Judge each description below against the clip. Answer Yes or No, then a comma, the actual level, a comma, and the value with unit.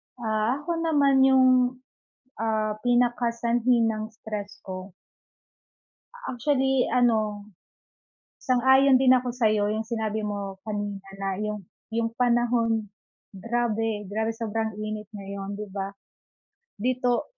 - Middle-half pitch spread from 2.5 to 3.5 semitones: Yes, average, 2.9 semitones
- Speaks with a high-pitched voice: Yes, high, 225 Hz